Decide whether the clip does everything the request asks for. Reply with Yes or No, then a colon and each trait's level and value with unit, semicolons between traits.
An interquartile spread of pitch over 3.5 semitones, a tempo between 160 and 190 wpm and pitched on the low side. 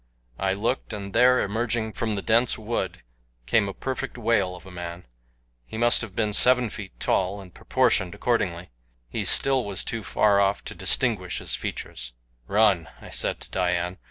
Yes: average, 4.1 semitones; average, 175 wpm; low, 100 Hz